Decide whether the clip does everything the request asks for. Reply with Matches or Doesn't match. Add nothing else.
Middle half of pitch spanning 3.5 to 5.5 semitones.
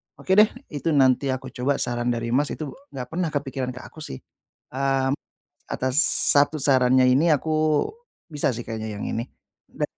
Doesn't match